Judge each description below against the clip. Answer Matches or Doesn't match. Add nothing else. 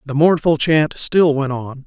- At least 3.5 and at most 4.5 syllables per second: Matches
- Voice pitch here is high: Doesn't match